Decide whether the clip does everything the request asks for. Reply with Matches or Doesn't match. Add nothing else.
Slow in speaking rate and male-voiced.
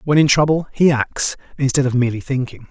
Doesn't match